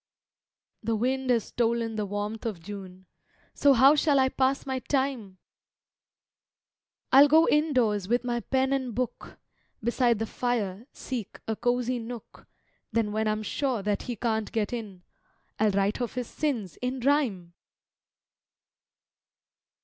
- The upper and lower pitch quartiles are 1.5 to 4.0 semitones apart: Yes, average, 3.7 semitones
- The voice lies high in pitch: Yes, high, 235 Hz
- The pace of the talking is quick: No, average, 140 wpm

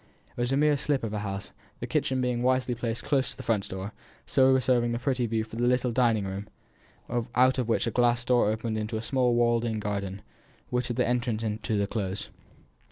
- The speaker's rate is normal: No, fast, 230 wpm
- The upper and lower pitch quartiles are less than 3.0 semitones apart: Yes, narrow, 2.5 semitones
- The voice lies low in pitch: Yes, low, 120 Hz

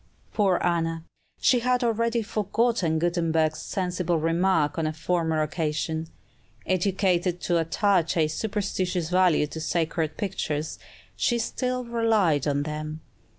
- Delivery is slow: Yes, slow, 120 wpm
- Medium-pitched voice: Yes, medium, 175 Hz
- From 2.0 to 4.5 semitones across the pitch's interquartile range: Yes, average, 4.1 semitones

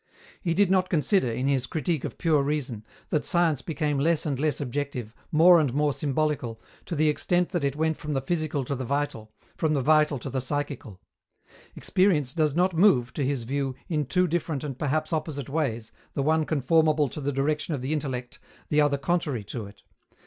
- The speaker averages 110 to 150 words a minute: No, average, 200 wpm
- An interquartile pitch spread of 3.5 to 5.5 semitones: No, average, 2.9 semitones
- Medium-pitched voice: Yes, medium, 145 Hz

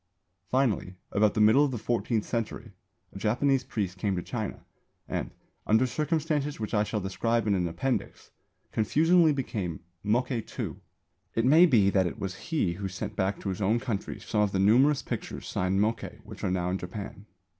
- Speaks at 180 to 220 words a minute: Yes, average, 185 wpm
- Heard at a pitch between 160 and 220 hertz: No, low, 110 Hz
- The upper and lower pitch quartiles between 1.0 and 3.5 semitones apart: No, average, 4.8 semitones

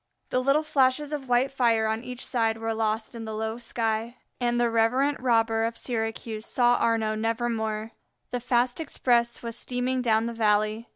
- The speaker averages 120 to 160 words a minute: No, average, 175 wpm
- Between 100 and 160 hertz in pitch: No, high, 230 Hz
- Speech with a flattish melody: Yes, narrow, 1.9 semitones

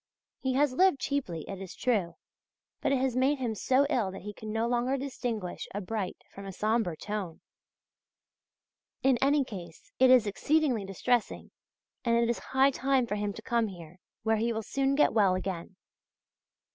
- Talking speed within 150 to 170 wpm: No, average, 180 wpm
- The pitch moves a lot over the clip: No, average, 4.9 semitones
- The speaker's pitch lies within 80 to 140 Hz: No, high, 230 Hz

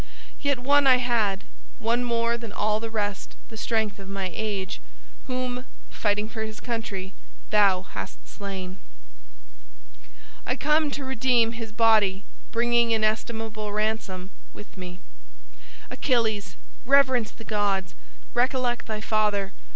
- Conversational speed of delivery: No, slow, 125 wpm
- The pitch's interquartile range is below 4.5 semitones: Yes, average, 2.8 semitones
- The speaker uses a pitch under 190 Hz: No, high, 220 Hz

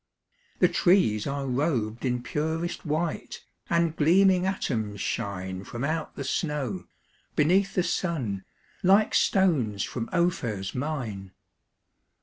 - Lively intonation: Yes, wide, 7.9 semitones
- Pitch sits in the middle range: Yes, medium, 145 Hz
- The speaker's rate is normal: No, slow, 115 wpm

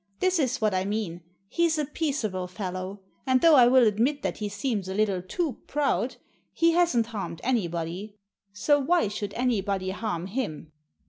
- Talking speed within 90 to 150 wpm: No, average, 170 wpm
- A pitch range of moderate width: No, wide, 6.1 semitones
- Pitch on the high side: Yes, high, 215 Hz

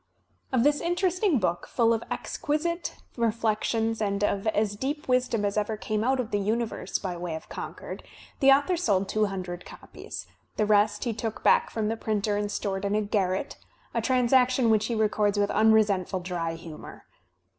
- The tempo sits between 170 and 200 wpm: Yes, average, 185 wpm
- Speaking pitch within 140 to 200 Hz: No, high, 215 Hz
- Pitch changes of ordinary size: Yes, average, 3.6 semitones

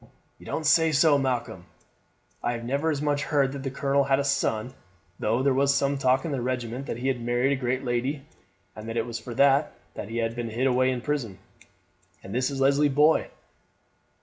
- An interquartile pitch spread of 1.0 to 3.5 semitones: Yes, narrow, 2.6 semitones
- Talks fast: Yes, fast, 210 wpm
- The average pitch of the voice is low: Yes, low, 130 Hz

